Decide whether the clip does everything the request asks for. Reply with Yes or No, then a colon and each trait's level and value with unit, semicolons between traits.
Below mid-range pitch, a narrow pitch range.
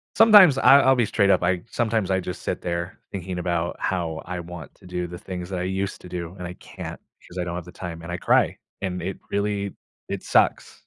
Yes: very low, 90 Hz; narrow, 2.2 semitones